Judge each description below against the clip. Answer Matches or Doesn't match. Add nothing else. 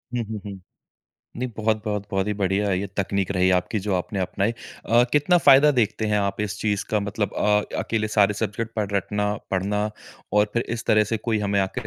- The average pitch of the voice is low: Matches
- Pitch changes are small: Matches